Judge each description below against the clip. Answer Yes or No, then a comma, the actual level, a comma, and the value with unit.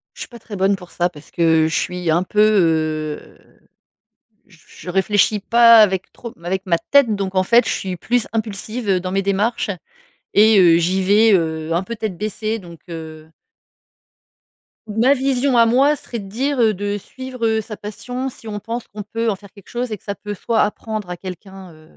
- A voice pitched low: No, high, 205 Hz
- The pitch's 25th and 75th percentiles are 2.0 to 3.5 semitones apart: No, average, 4.0 semitones